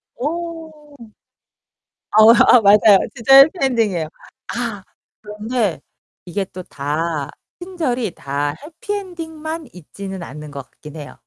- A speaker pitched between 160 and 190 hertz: No, high, 220 Hz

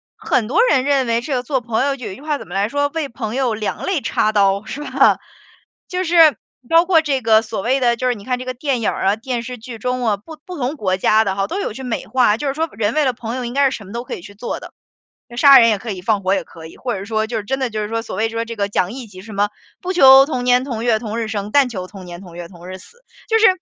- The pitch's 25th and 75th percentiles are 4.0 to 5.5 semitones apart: Yes, average, 4.3 semitones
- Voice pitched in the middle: No, high, 235 Hz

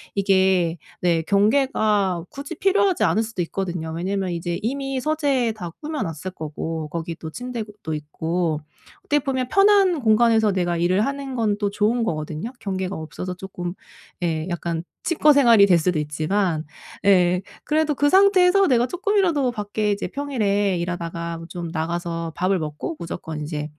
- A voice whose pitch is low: No, high, 195 Hz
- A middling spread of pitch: No, wide, 7.3 semitones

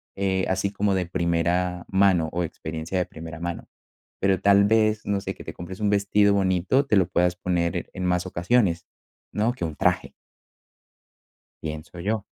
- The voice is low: Yes, very low, 95 Hz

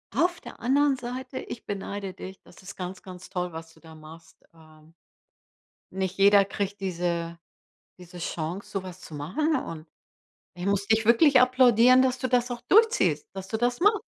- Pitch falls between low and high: No, high, 195 Hz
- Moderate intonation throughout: No, wide, 6.1 semitones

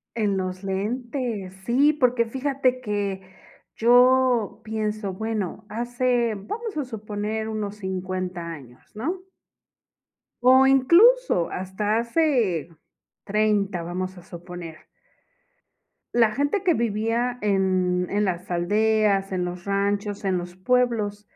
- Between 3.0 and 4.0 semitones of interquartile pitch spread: No, average, 4.5 semitones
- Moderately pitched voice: No, high, 210 Hz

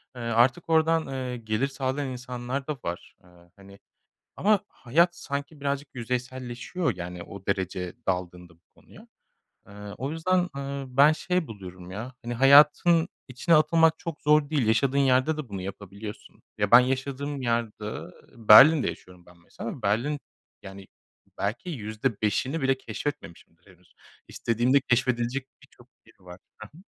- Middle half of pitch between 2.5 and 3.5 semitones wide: No, wide, 5.5 semitones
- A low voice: Yes, low, 125 Hz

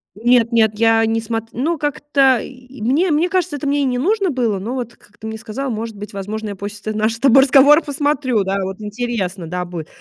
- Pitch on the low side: No, high, 235 Hz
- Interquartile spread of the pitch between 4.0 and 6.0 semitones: Yes, average, 4.5 semitones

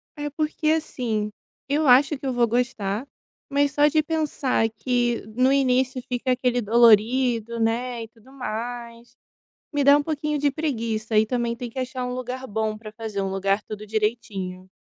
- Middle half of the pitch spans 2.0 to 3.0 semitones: No, average, 3.4 semitones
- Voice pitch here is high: Yes, high, 245 Hz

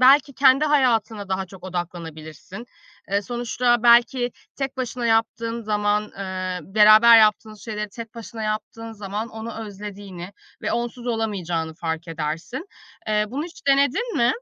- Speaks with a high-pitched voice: Yes, high, 220 Hz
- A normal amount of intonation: Yes, average, 3.8 semitones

